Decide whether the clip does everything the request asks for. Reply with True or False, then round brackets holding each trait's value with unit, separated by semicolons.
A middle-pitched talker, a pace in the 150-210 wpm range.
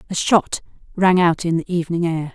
True (170 Hz; 205 wpm)